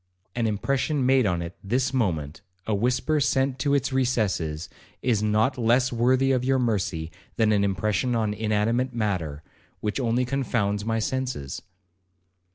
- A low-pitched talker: Yes, low, 115 Hz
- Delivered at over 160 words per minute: No, average, 150 wpm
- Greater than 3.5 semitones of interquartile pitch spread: Yes, average, 4.1 semitones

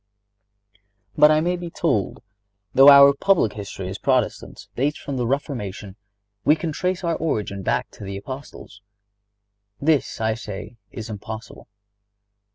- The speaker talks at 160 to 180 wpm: No, average, 140 wpm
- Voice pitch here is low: Yes, low, 130 Hz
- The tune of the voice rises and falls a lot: Yes, wide, 6.6 semitones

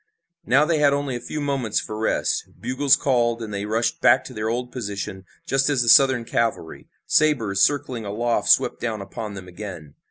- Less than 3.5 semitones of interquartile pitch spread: No, average, 4.2 semitones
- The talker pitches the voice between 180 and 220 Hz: No, low, 120 Hz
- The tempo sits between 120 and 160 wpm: No, average, 190 wpm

